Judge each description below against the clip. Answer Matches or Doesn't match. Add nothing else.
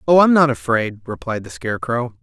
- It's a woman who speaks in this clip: Doesn't match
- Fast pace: Doesn't match